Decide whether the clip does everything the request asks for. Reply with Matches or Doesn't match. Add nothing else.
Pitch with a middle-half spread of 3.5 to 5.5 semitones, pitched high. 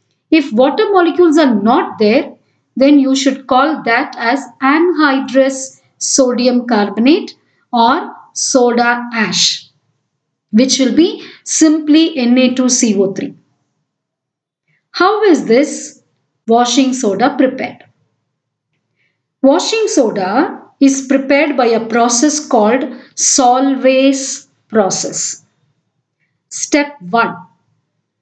Matches